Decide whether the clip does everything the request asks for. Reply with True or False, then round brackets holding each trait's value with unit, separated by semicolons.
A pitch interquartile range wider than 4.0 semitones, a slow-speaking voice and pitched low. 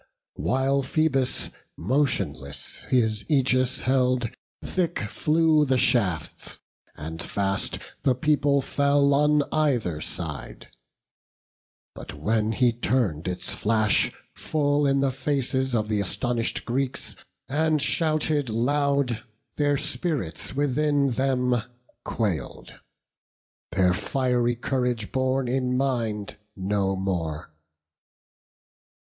True (4.6 semitones; 100 wpm; 130 Hz)